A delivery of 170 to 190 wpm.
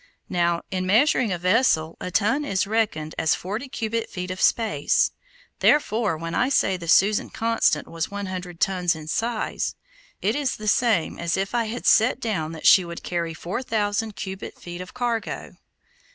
Yes: average, 180 wpm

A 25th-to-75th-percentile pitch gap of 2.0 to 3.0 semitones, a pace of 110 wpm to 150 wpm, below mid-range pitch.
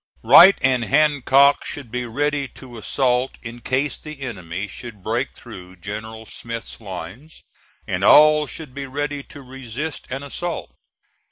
No: average, 4.1 semitones; average, 145 wpm; low, 130 Hz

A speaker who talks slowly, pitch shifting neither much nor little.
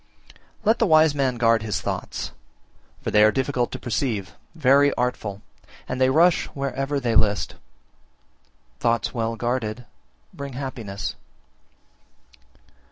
Yes: slow, 125 wpm; average, 3.6 semitones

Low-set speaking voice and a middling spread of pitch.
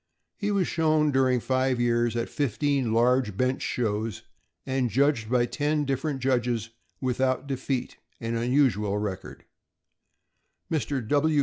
Yes: low, 130 Hz; average, 3.1 semitones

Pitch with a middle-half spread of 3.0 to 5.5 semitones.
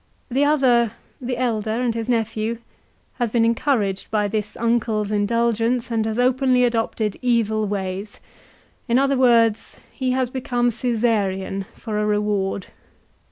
No: narrow, 2.6 semitones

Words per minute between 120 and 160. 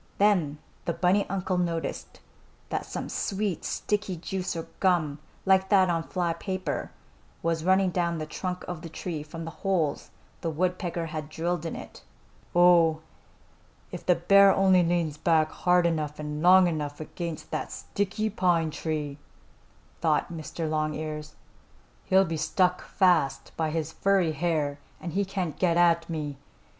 Yes: average, 150 wpm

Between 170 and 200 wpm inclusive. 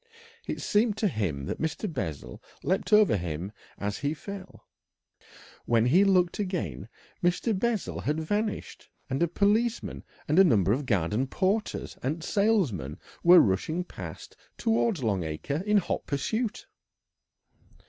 No: average, 140 wpm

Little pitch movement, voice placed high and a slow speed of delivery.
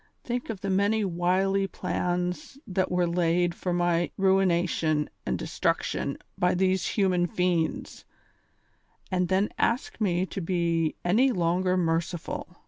No: narrow, 1.8 semitones; medium, 180 Hz; slow, 130 wpm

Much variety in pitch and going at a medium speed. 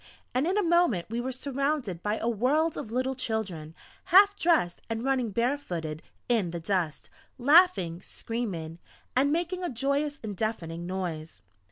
Yes: wide, 8.1 semitones; average, 160 wpm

